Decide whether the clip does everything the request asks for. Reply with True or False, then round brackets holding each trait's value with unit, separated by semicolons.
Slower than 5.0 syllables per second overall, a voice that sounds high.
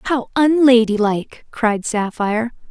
True (4.1 syllables/s; 230 Hz)